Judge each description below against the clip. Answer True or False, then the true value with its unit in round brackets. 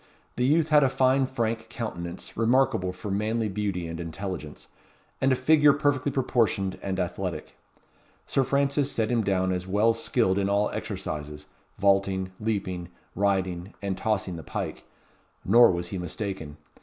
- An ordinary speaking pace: True (150 wpm)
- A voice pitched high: False (100 Hz)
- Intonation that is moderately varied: True (4.8 semitones)